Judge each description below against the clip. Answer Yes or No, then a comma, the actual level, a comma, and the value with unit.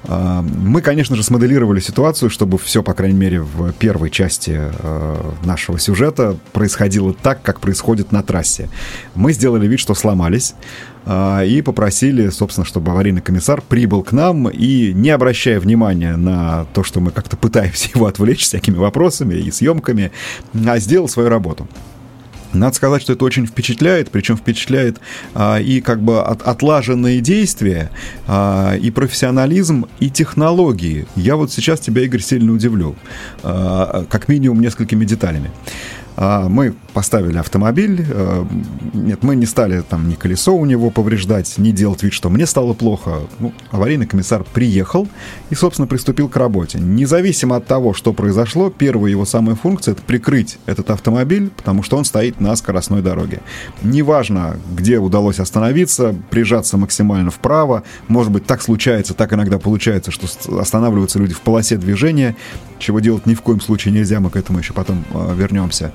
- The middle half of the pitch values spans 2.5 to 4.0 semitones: No, average, 4.7 semitones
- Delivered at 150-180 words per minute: Yes, average, 155 wpm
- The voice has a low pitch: Yes, low, 110 Hz